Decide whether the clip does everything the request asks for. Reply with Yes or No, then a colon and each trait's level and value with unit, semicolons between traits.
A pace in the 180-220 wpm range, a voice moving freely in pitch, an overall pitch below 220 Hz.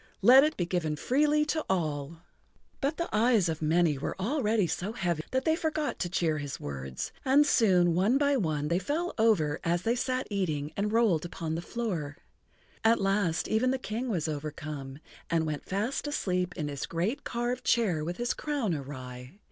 Yes: average, 185 wpm; wide, 7.6 semitones; medium, 185 Hz